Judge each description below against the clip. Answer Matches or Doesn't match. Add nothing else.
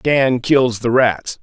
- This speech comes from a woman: Doesn't match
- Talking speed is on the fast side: Doesn't match